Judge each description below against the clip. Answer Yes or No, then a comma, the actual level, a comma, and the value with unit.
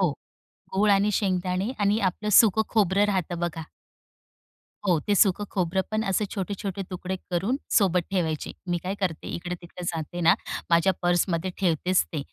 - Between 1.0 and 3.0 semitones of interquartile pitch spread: Yes, narrow, 2.4 semitones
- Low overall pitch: No, medium, 185 Hz